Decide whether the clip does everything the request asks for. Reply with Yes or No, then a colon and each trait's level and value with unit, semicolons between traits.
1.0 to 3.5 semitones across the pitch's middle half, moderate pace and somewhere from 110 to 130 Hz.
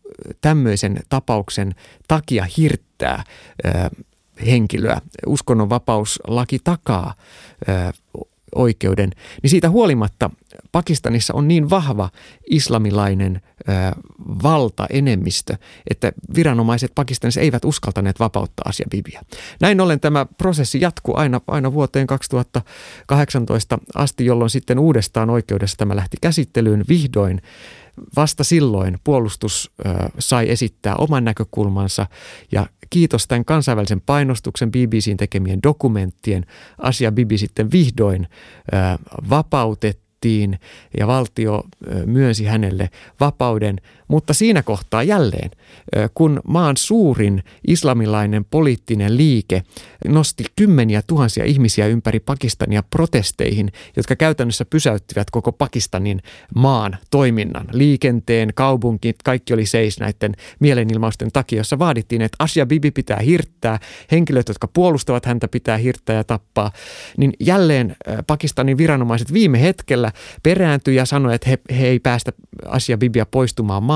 No: average, 5.1 semitones; average, 110 wpm; low, 120 Hz